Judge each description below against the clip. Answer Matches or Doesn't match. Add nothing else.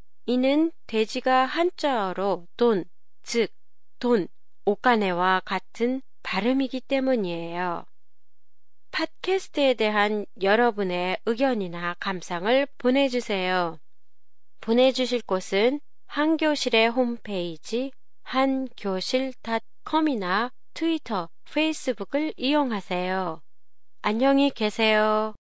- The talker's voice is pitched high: Matches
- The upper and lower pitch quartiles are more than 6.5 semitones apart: Doesn't match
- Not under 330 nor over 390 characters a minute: Doesn't match